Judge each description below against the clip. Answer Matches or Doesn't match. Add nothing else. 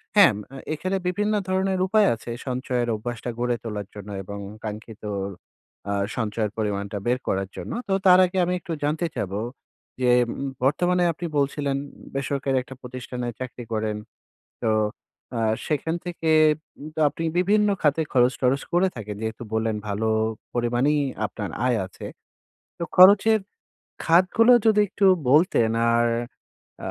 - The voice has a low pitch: Matches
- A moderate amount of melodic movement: Doesn't match